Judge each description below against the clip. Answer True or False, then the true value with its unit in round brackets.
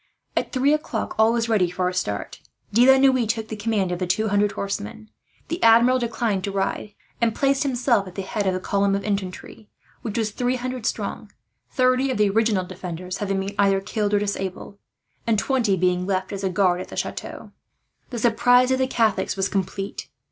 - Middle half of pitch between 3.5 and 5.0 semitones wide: True (3.8 semitones)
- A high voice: True (210 Hz)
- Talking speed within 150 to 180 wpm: False (205 wpm)